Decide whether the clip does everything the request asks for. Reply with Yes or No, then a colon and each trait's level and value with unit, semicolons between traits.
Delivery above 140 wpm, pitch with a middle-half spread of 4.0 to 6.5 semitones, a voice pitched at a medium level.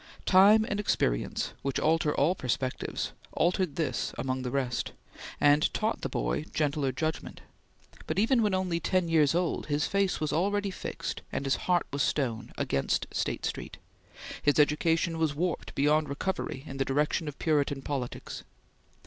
Yes: average, 155 wpm; average, 4.5 semitones; medium, 150 Hz